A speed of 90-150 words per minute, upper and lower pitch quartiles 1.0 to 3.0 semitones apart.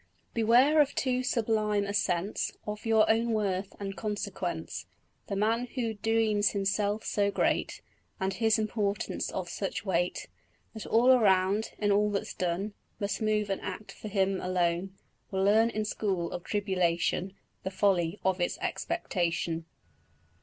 Yes: average, 145 wpm; average, 2.7 semitones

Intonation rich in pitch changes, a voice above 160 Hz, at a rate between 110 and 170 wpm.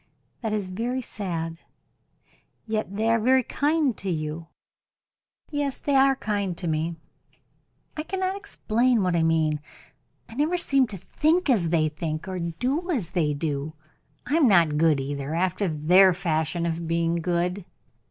Yes: wide, 7.6 semitones; medium, 185 Hz; average, 155 wpm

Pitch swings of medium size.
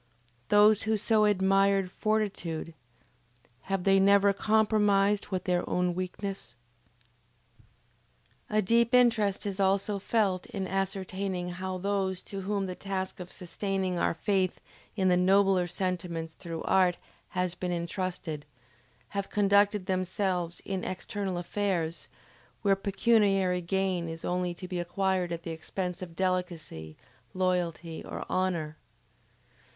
No: narrow, 2.0 semitones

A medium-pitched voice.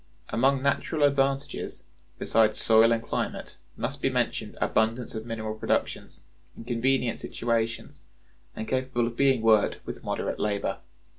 No: low, 115 Hz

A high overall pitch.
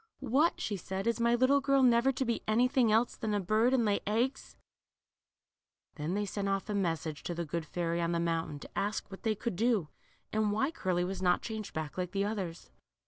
Yes: high, 205 Hz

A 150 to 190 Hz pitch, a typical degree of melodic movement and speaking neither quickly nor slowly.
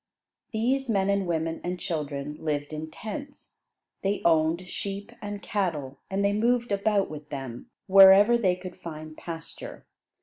Yes: medium, 185 Hz; average, 4.6 semitones; average, 145 wpm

